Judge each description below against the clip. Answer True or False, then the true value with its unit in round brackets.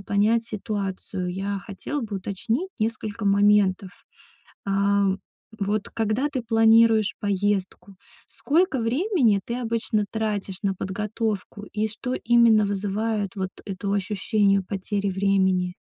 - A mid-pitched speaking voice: False (205 Hz)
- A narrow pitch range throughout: True (2.3 semitones)